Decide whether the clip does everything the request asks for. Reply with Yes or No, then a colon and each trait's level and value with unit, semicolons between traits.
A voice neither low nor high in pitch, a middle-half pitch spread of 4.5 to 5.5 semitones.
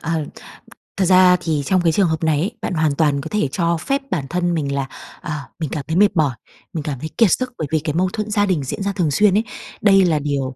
No: medium, 165 Hz; average, 4.1 semitones